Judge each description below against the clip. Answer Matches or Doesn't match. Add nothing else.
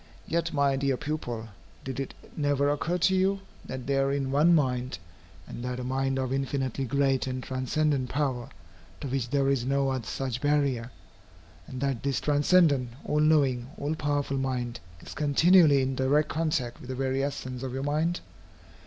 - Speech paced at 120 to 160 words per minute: Doesn't match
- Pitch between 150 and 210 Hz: Doesn't match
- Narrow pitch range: Matches